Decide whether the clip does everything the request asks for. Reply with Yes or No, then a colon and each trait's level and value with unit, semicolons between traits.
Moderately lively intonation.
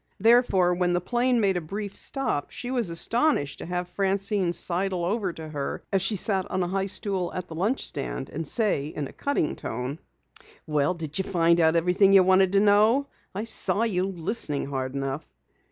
Yes: average, 3.8 semitones